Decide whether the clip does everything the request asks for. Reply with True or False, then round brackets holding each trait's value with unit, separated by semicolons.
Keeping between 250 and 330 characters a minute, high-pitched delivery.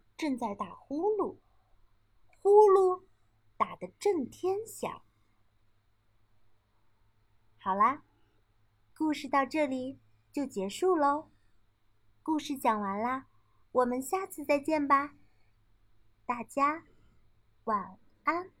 False (125 characters per minute; 245 Hz)